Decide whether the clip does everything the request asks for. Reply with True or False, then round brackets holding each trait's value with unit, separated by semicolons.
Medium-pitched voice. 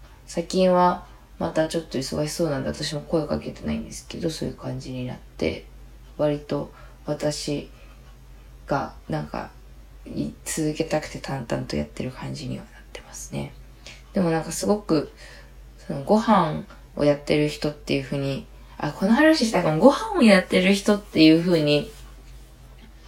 True (150 Hz)